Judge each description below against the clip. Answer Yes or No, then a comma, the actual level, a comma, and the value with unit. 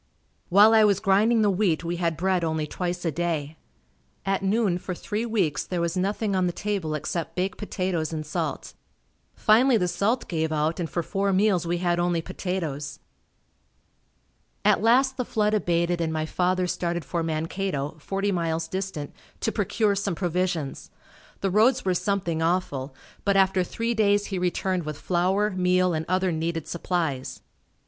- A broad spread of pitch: No, average, 3.1 semitones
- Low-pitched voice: No, medium, 180 Hz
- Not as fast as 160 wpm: No, average, 170 wpm